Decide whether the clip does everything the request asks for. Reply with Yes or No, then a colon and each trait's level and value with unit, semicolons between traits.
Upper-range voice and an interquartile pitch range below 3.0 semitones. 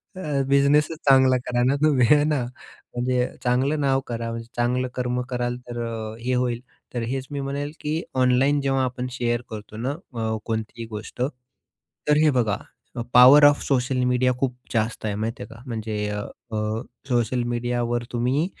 No: low, 125 Hz; narrow, 2.5 semitones